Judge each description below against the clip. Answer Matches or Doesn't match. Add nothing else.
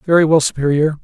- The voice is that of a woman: Doesn't match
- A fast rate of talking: Doesn't match